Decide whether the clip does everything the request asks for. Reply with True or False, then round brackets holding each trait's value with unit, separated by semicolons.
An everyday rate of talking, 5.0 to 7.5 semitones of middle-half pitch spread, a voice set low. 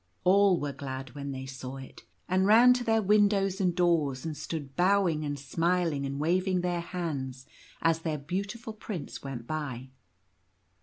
False (160 wpm; 5.4 semitones; 165 Hz)